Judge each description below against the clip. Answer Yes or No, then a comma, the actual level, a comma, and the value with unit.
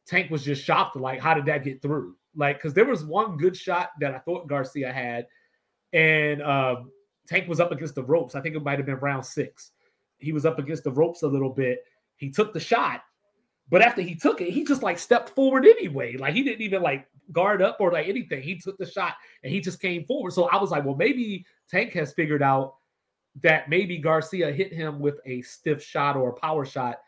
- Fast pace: Yes, fast, 230 wpm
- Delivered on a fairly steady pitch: No, average, 4.7 semitones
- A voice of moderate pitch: Yes, medium, 160 Hz